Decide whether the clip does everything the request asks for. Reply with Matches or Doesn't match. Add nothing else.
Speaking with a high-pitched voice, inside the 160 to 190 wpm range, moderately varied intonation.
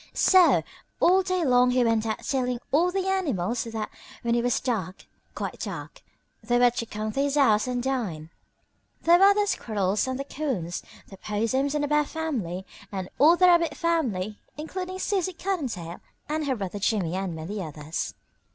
Doesn't match